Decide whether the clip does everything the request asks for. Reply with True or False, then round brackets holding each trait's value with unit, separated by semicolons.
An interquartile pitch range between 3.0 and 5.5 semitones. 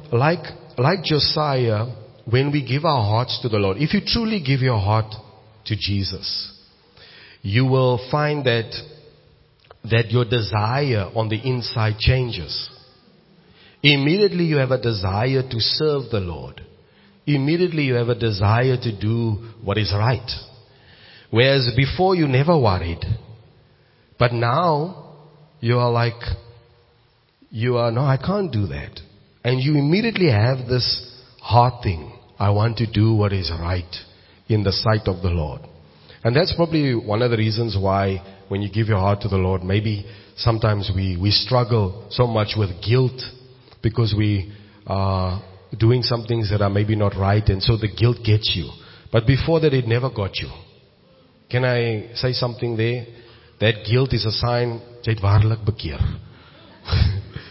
True (3.7 semitones)